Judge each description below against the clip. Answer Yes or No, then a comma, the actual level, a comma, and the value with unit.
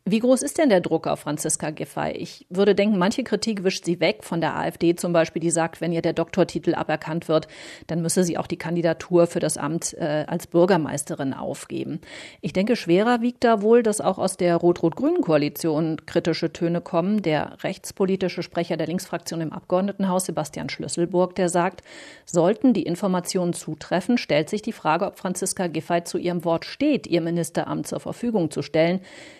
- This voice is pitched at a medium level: Yes, medium, 175 Hz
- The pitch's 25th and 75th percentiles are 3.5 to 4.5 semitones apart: No, average, 3.0 semitones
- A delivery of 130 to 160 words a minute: No, average, 180 wpm